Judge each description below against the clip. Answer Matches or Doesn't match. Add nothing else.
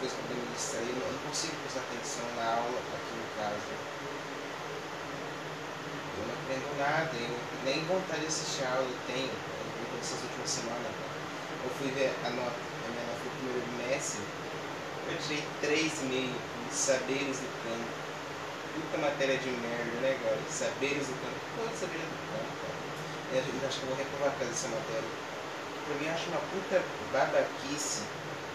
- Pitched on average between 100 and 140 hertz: Matches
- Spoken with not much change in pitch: Matches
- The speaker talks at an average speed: Matches